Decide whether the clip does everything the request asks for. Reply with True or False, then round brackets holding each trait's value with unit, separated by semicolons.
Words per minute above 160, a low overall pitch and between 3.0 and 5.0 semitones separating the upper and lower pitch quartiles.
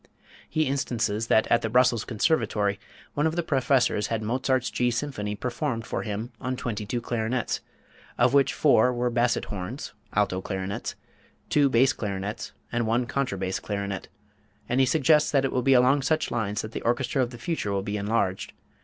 True (185 wpm; 120 Hz; 3.9 semitones)